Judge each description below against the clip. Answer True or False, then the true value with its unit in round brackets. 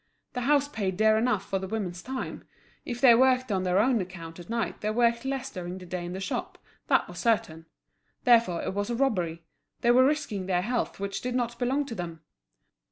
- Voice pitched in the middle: False (220 Hz)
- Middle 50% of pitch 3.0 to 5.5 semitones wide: True (5.2 semitones)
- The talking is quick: True (215 wpm)